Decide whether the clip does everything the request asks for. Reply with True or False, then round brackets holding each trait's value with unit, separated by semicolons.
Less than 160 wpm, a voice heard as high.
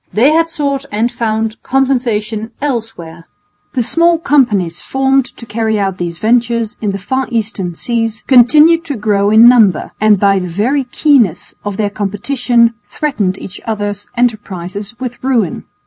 True (150 wpm; 225 Hz)